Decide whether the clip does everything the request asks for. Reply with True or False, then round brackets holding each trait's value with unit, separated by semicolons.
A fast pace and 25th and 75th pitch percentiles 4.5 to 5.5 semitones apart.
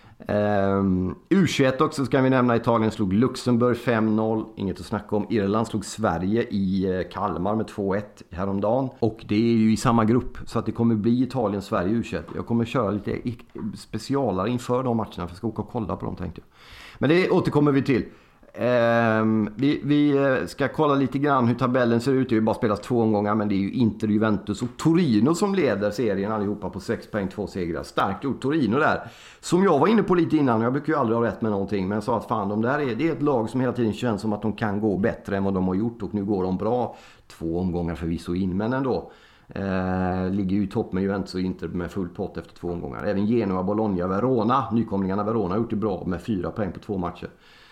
False (230 wpm; 3.7 semitones)